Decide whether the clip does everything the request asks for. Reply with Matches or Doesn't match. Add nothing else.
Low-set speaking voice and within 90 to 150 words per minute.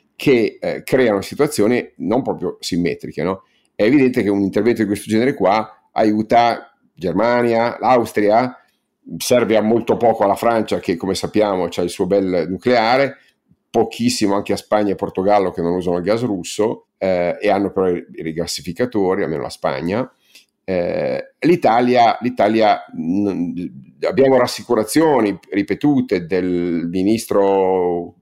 Matches